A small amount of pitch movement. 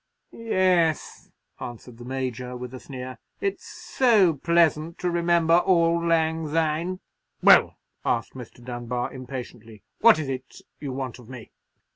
No: average, 5.2 semitones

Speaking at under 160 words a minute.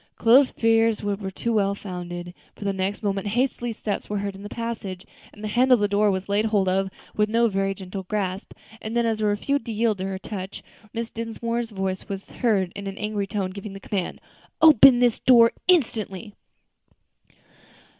No: average, 195 wpm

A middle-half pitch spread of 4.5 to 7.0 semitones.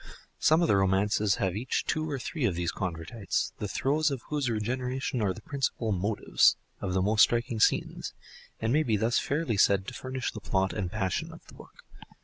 Yes: average, 4.9 semitones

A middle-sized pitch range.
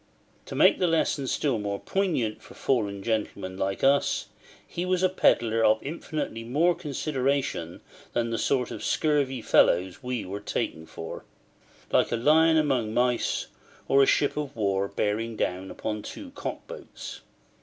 No: wide, 5.9 semitones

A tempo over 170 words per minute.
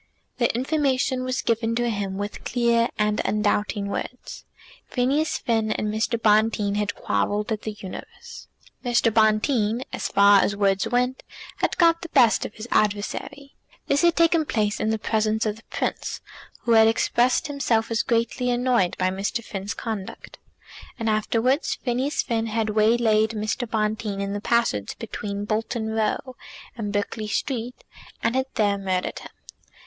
No: average, 155 wpm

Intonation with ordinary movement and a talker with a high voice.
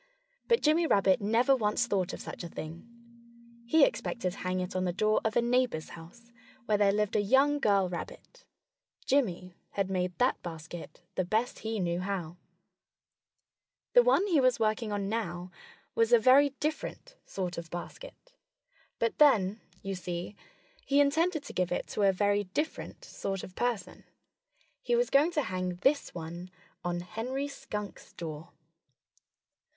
No: wide, 6.5 semitones; high, 210 Hz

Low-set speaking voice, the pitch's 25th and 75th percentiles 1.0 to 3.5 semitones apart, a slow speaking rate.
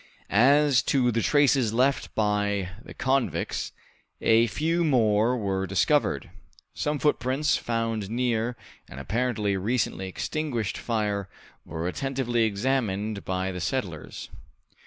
No: low, 115 Hz; average, 4.6 semitones; slow, 115 wpm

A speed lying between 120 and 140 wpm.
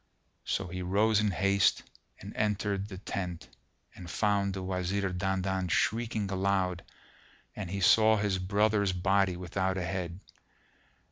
Yes: slow, 135 wpm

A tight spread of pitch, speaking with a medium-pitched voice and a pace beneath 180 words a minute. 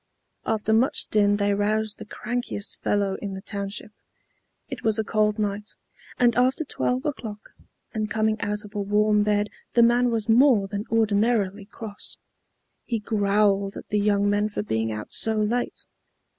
No: narrow, 1.6 semitones; high, 210 Hz; average, 165 wpm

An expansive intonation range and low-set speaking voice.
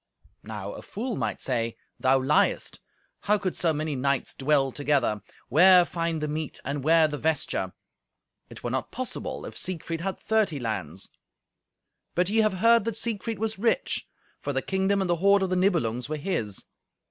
No: wide, 6.3 semitones; medium, 160 Hz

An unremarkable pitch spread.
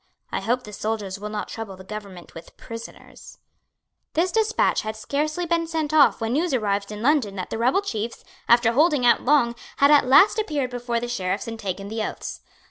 No: wide, 5.9 semitones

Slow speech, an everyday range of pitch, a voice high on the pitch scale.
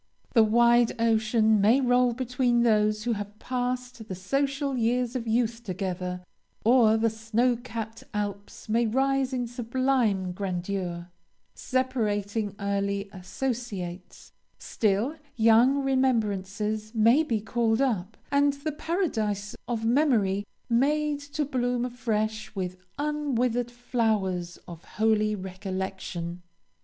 Yes: slow, 115 wpm; average, 3.6 semitones; high, 225 Hz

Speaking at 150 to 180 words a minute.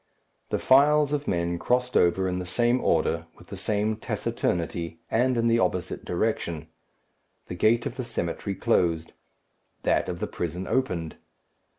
Yes: average, 155 wpm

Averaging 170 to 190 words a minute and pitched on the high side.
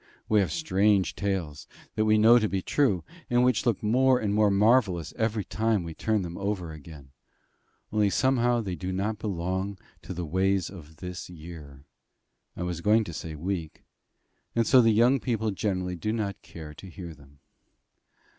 No: average, 175 wpm; low, 100 Hz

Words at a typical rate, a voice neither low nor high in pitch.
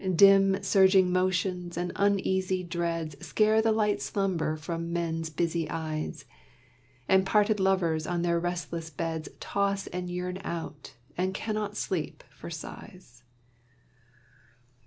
No: slow, 120 wpm; medium, 180 Hz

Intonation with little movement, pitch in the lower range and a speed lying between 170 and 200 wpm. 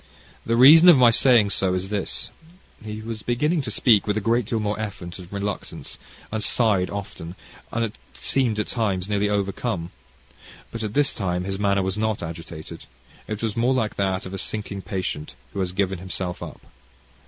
No: average, 3.2 semitones; low, 105 Hz; average, 190 wpm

